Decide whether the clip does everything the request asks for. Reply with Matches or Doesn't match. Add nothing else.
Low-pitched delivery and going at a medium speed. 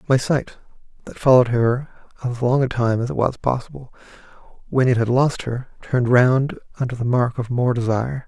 Matches